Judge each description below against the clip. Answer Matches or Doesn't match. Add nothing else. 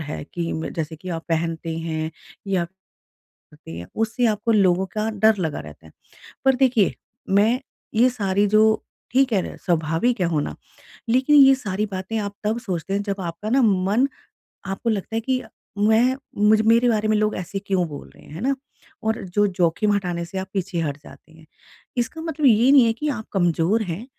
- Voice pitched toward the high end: Matches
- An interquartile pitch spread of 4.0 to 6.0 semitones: Matches